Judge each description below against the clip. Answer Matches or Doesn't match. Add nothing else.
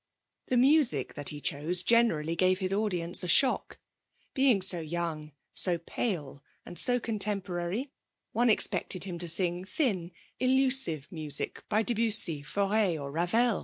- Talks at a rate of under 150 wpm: Matches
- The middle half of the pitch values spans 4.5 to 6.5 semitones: Matches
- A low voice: Doesn't match